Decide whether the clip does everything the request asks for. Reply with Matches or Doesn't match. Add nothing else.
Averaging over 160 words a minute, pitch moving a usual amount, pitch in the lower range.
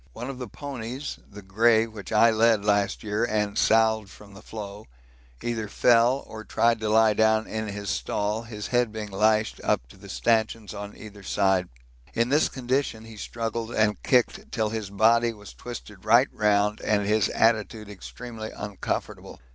Doesn't match